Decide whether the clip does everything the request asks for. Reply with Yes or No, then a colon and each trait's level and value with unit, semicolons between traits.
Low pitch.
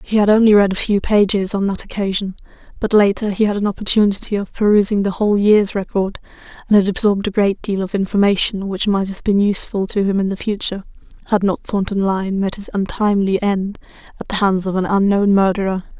No: high, 200 Hz